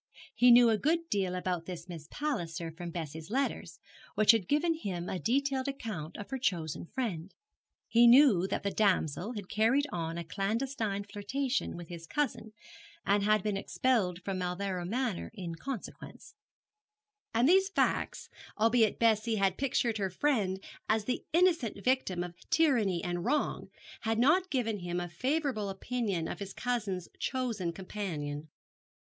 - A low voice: No, high, 210 Hz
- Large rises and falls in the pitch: Yes, wide, 5.9 semitones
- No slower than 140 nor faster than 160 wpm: Yes, average, 155 wpm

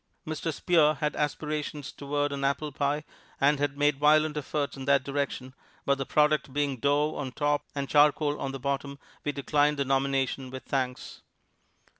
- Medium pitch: Yes, medium, 145 Hz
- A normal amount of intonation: No, narrow, 1.5 semitones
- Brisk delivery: No, average, 170 wpm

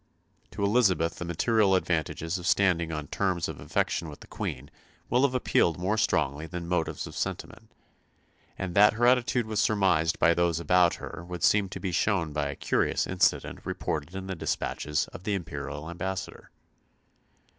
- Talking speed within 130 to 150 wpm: No, average, 170 wpm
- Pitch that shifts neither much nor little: Yes, average, 3.6 semitones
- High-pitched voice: No, very low, 90 Hz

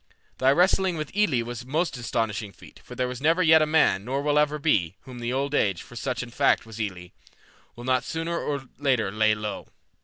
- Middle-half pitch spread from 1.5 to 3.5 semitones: No, average, 5.2 semitones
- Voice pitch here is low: Yes, low, 130 Hz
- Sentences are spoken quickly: Yes, fast, 220 wpm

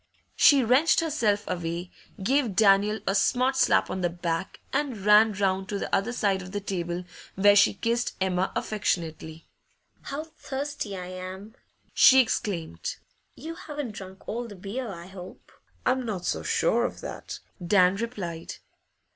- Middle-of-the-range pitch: No, high, 200 Hz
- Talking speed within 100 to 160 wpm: Yes, average, 155 wpm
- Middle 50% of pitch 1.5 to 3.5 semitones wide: No, average, 4.8 semitones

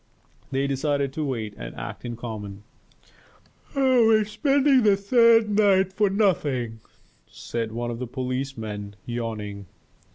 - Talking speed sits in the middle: No, slow, 130 wpm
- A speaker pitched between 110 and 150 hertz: Yes, low, 135 Hz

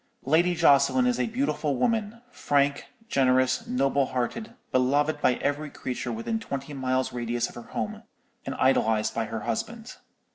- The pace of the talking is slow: No, average, 150 wpm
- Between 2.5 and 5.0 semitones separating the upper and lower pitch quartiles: No, wide, 5.6 semitones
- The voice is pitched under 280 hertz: Yes, medium, 140 Hz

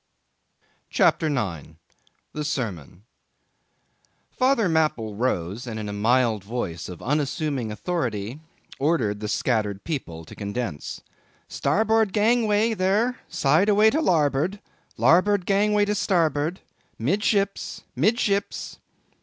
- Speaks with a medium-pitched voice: Yes, medium, 150 Hz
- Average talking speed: No, slow, 105 wpm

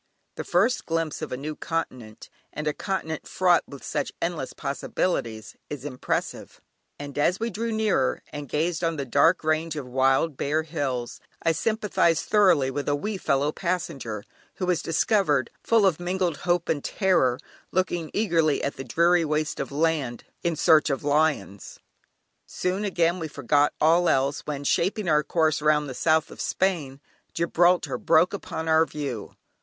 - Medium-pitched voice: Yes, medium, 160 Hz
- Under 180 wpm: Yes, average, 165 wpm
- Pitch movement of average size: Yes, average, 3.7 semitones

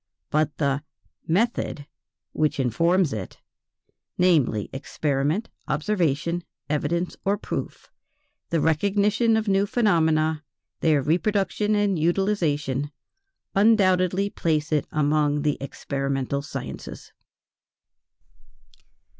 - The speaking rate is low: Yes, slow, 90 wpm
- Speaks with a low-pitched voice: No, medium, 160 Hz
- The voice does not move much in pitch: No, average, 5.1 semitones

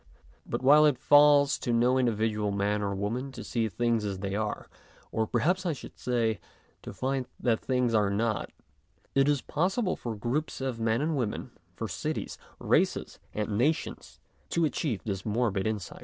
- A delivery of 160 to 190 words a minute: Yes, average, 170 wpm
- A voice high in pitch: No, low, 120 Hz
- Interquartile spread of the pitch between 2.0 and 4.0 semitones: No, average, 4.5 semitones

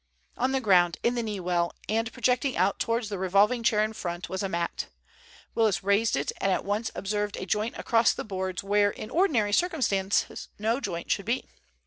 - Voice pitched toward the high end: Yes, high, 210 Hz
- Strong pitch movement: No, average, 3.3 semitones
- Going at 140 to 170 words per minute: No, average, 195 wpm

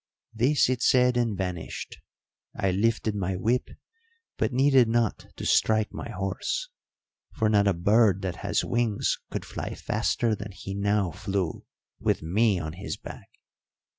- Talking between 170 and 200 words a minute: No, average, 150 wpm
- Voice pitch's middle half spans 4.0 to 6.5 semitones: No, average, 3.5 semitones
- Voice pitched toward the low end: Yes, low, 105 Hz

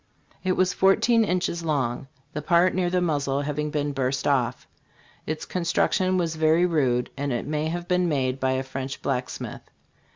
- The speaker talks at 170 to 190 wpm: Yes, average, 175 wpm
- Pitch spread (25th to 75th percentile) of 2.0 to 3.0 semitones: No, average, 4.6 semitones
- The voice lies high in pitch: No, medium, 150 Hz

